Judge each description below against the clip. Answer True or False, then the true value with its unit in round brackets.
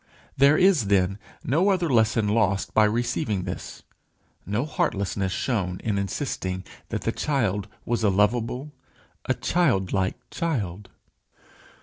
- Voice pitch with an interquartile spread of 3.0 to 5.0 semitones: False (5.6 semitones)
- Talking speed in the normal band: False (120 wpm)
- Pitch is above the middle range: False (110 Hz)